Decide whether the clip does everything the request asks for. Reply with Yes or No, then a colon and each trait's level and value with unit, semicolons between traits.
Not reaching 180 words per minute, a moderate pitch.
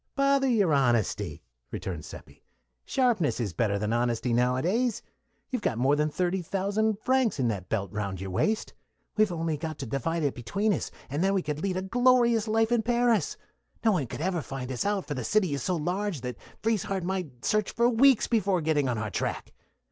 No: average, 200 wpm; medium, 175 Hz